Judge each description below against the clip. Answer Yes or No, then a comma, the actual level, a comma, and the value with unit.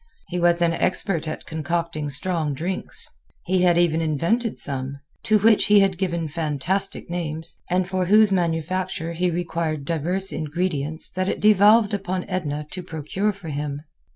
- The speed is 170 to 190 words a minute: No, average, 155 wpm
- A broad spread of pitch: No, average, 3.1 semitones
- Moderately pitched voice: Yes, medium, 175 Hz